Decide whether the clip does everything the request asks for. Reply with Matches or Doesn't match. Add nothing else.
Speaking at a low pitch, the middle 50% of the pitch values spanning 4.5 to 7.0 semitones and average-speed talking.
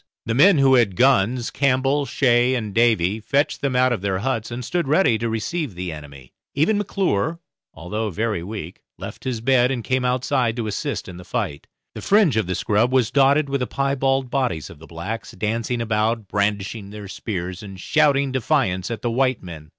Matches